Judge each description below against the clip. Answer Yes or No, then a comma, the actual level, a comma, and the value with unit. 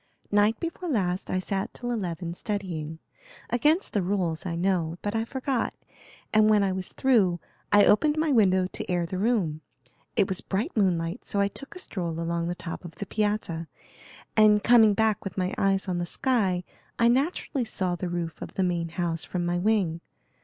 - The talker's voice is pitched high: Yes, high, 195 Hz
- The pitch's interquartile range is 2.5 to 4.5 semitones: Yes, average, 3.9 semitones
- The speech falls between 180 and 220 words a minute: Yes, average, 190 wpm